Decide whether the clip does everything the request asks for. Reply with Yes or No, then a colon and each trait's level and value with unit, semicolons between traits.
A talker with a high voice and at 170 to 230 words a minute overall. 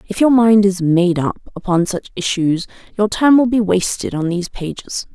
Yes: high, 195 Hz; average, 200 wpm